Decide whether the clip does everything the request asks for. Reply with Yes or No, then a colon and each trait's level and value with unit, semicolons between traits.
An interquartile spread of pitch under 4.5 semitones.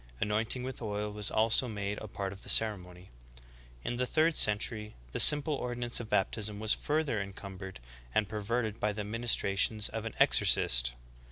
Yes: average, 2.8 semitones